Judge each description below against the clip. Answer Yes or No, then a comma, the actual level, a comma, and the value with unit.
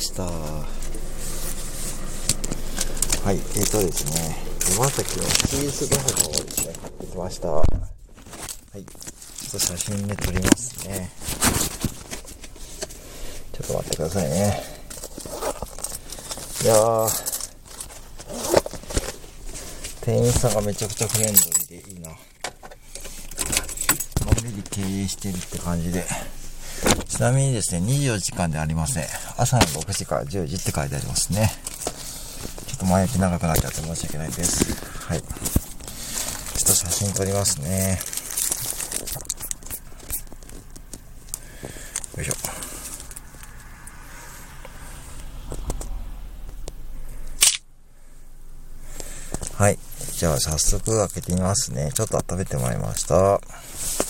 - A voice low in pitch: Yes, very low, 95 Hz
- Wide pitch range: No, average, 4.0 semitones